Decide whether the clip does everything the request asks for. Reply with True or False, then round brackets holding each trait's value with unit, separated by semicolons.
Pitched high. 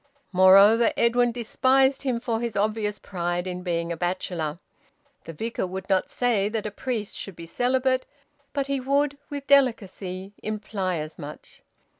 True (210 Hz)